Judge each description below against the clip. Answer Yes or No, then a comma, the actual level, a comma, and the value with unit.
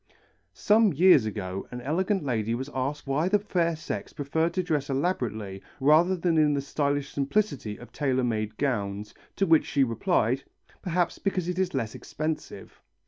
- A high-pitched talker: No, medium, 145 Hz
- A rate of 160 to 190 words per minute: Yes, average, 165 wpm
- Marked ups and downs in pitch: Yes, wide, 6.0 semitones